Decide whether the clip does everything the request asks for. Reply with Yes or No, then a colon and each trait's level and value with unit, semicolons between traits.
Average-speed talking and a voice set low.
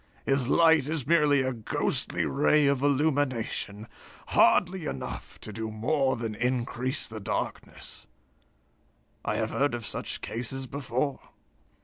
No: slow, 125 wpm; low, 130 Hz